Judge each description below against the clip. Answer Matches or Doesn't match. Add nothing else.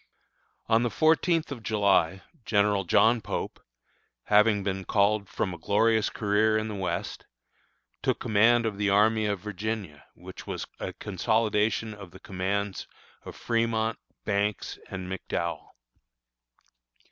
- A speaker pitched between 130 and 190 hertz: Doesn't match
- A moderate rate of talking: Doesn't match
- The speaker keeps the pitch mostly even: Matches